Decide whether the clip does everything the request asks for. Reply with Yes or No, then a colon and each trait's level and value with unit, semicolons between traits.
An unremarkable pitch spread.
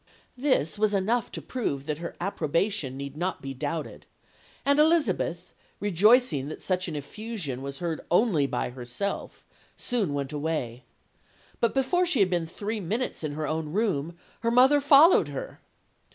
No: wide, 7.6 semitones